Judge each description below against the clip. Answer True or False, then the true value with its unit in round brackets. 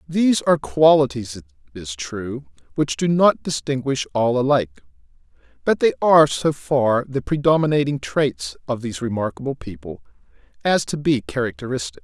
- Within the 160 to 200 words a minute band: False (140 wpm)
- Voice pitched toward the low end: True (130 Hz)